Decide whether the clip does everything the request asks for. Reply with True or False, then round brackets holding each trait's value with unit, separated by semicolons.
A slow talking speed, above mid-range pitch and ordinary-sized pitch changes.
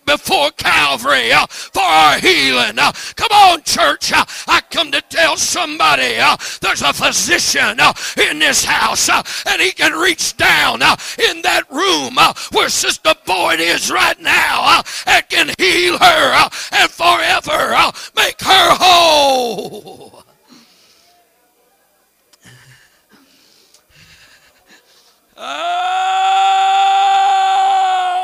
True (115 wpm; 355 Hz; 3.2 semitones)